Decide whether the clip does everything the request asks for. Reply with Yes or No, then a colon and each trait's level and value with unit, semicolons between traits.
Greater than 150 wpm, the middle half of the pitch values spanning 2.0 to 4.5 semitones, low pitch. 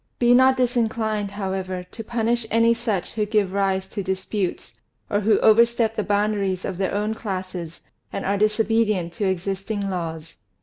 No: average, 160 wpm; average, 2.9 semitones; high, 205 Hz